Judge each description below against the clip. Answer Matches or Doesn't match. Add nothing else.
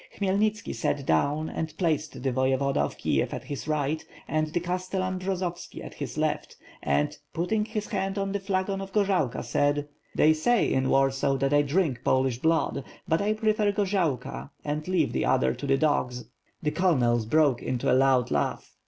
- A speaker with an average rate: Matches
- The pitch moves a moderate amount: Doesn't match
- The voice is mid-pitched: Matches